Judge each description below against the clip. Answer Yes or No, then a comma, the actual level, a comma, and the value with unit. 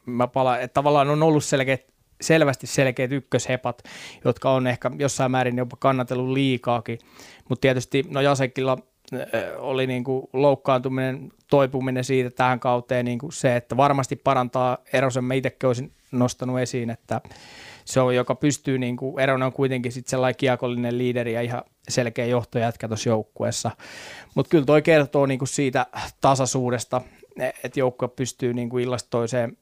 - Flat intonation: Yes, narrow, 1.4 semitones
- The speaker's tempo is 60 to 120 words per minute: No, average, 140 wpm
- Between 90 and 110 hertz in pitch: No, low, 130 Hz